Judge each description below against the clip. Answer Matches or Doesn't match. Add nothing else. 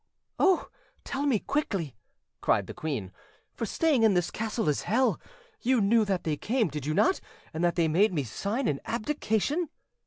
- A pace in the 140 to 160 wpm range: Doesn't match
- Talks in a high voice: Matches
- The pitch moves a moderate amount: Doesn't match